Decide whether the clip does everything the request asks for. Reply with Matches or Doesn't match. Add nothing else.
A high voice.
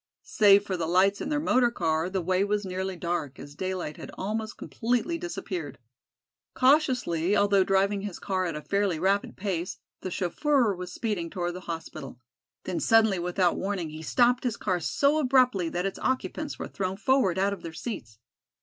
Matches